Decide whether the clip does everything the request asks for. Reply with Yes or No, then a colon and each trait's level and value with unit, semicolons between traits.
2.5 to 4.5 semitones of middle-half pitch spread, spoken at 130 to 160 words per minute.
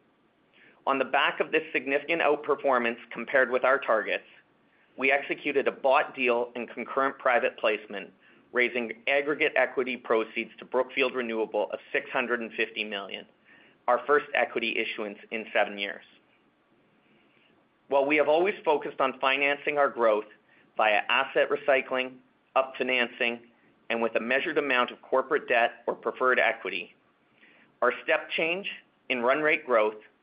Yes: average, 2.9 semitones; slow, 135 wpm